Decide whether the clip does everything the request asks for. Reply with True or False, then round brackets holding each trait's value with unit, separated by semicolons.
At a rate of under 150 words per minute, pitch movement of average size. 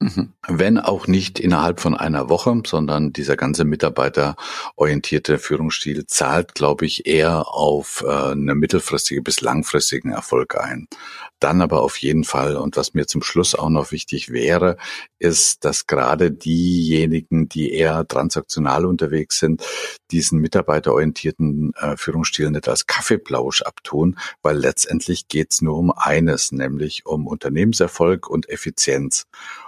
False (135 wpm; 2.1 semitones)